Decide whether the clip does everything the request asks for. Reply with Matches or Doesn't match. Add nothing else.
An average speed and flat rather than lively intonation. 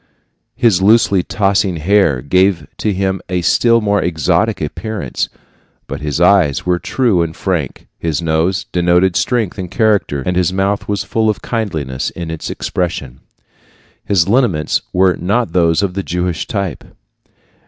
Doesn't match